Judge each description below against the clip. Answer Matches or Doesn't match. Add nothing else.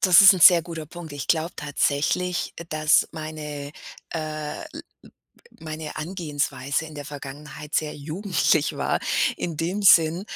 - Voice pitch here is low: Doesn't match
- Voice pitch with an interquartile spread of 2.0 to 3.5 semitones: Matches